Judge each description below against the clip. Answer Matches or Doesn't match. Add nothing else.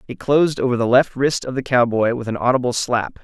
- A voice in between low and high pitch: Doesn't match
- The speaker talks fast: Matches